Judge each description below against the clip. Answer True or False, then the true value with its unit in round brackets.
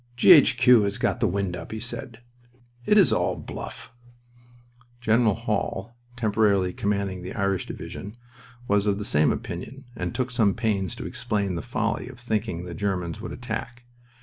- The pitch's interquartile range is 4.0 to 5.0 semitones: False (3.6 semitones)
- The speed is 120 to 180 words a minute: True (160 wpm)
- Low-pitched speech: True (105 Hz)